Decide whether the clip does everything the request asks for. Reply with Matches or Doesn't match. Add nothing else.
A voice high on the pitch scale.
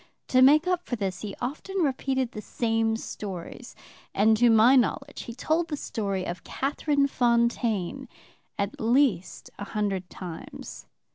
Matches